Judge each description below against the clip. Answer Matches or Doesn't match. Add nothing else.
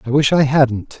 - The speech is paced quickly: Matches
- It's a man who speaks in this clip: Matches